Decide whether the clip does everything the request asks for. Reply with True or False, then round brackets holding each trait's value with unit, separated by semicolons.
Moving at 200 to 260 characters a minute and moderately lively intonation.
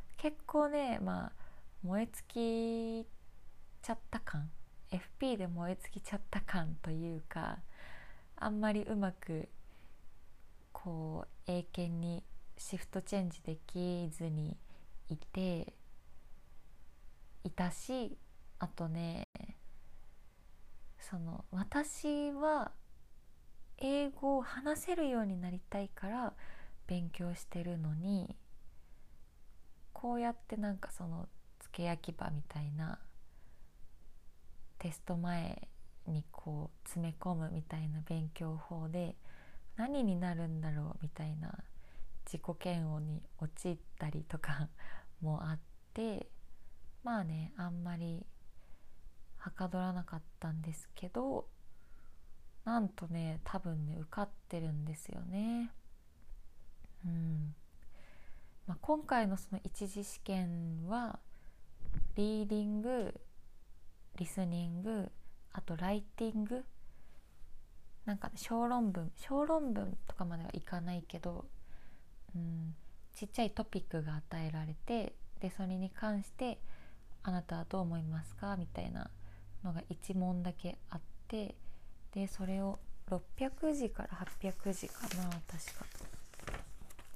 True (205 characters per minute; 4.6 semitones)